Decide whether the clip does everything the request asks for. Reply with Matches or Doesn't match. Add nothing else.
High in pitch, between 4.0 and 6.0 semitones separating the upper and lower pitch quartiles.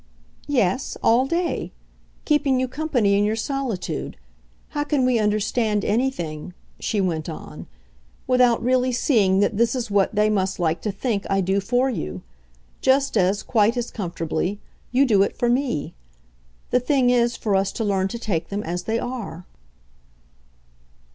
Matches